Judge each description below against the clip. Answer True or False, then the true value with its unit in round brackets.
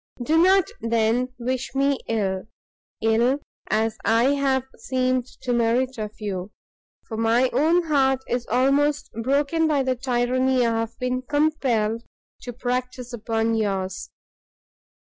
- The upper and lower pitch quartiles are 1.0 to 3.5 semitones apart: True (2.9 semitones)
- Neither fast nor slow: False (130 wpm)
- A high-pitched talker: True (250 Hz)